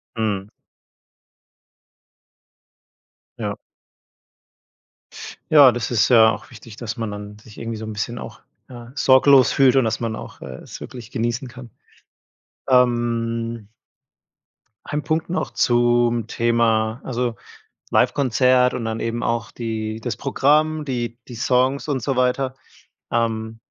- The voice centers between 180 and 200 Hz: No, low, 120 Hz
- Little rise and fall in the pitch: Yes, narrow, 2.2 semitones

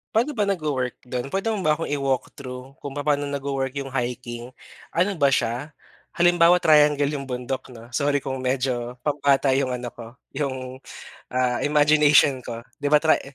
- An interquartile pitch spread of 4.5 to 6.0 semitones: No, average, 2.8 semitones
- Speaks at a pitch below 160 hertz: Yes, medium, 140 Hz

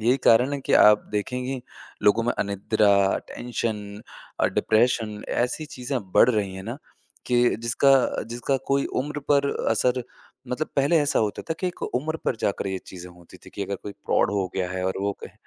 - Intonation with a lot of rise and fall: No, average, 4.3 semitones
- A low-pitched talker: Yes, low, 115 Hz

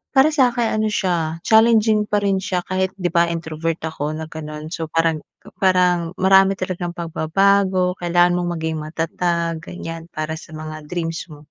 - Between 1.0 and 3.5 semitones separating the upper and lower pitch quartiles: Yes, average, 2.9 semitones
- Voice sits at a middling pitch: Yes, medium, 175 Hz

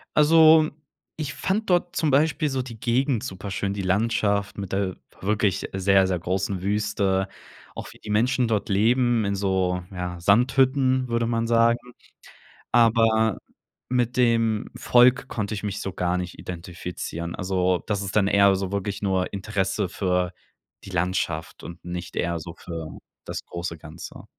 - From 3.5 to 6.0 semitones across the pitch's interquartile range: Yes, average, 4.2 semitones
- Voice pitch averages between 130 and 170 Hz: No, low, 100 Hz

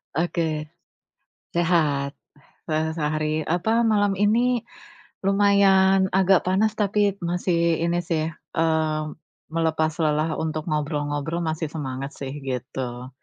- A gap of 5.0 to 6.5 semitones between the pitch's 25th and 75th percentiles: No, average, 3.8 semitones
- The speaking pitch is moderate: Yes, medium, 165 Hz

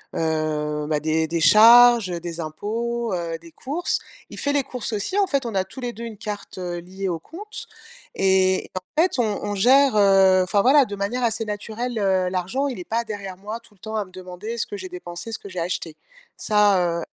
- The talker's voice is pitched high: Yes, high, 200 Hz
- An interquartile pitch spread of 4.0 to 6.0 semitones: Yes, average, 4.5 semitones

